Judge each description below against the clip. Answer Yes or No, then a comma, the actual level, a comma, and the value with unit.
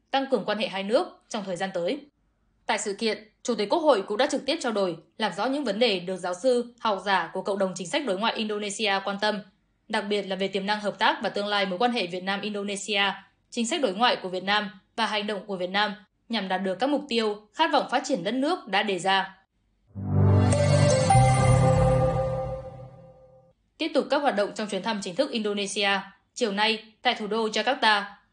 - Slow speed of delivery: No, average, 220 wpm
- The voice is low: No, high, 205 Hz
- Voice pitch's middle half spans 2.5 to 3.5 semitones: Yes, average, 3.2 semitones